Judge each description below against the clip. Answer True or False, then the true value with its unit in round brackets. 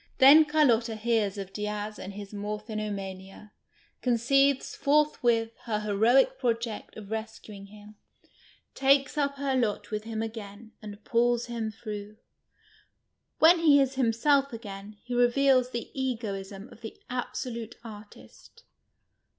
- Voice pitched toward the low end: False (225 Hz)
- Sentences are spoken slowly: True (125 wpm)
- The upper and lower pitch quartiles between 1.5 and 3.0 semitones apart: False (3.6 semitones)